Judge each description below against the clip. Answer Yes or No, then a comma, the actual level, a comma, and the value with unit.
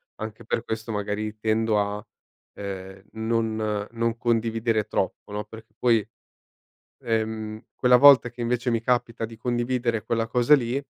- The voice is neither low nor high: No, low, 115 Hz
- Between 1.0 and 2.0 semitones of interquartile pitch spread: Yes, narrow, 1.7 semitones